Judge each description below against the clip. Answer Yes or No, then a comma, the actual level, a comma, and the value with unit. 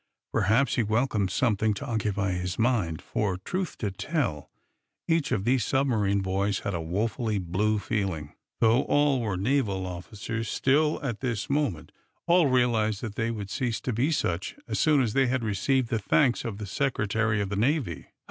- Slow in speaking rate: No, average, 175 wpm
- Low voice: Yes, low, 110 Hz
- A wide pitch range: No, average, 4.8 semitones